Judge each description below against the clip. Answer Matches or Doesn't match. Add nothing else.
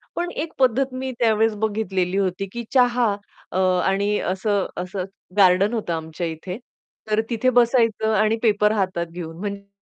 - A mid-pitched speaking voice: Doesn't match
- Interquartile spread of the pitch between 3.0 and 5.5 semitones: Matches